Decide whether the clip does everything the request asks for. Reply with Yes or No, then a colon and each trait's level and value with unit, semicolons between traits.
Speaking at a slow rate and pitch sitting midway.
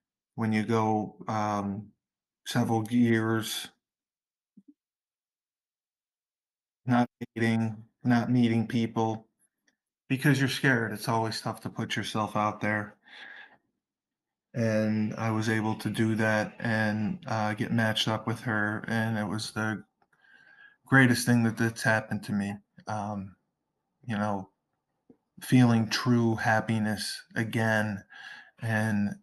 No: slow, 110 wpm; low, 110 Hz